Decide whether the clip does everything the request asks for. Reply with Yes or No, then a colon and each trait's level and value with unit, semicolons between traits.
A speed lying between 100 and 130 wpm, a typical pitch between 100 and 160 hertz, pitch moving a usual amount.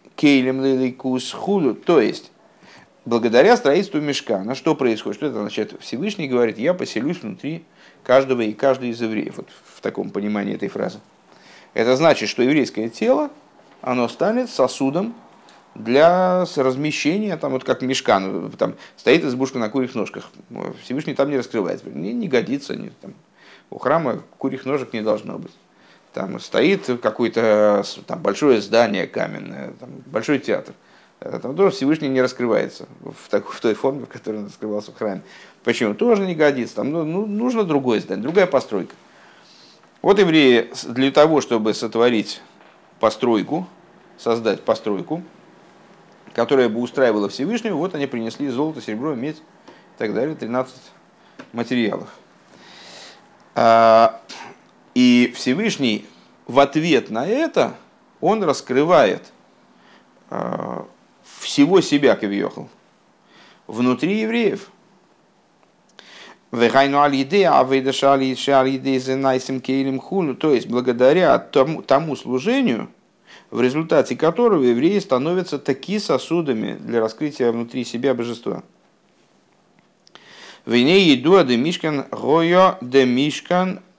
No: average, 115 wpm; low, 135 Hz; wide, 6.1 semitones